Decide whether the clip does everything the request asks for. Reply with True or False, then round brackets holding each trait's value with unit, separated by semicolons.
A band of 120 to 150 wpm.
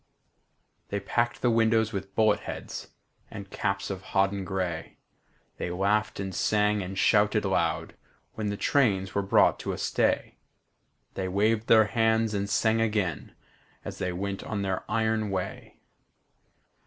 True (145 wpm)